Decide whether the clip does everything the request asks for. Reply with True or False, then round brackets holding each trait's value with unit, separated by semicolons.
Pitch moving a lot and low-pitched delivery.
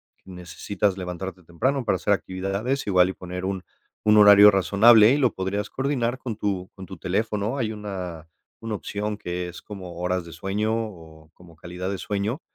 False (2.9 semitones; 100 Hz)